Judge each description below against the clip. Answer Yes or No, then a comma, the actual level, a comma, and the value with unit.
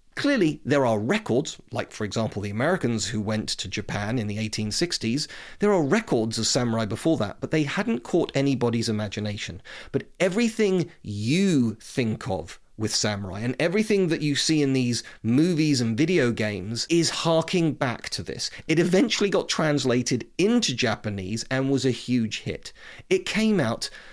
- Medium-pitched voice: No, low, 125 Hz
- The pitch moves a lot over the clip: Yes, wide, 7.1 semitones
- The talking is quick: No, average, 165 wpm